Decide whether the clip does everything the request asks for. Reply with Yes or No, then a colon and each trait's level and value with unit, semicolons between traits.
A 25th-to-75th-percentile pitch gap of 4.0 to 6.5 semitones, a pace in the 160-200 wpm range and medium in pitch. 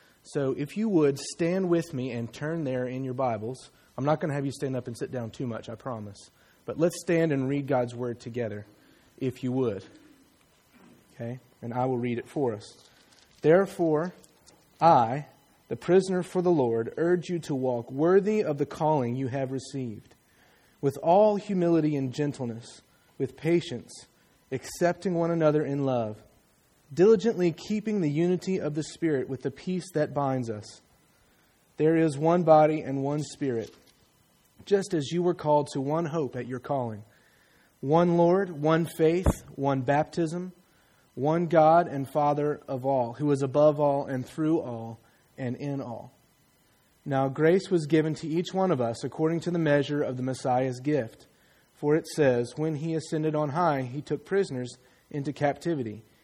Yes: average, 4.3 semitones; average, 170 wpm; medium, 145 Hz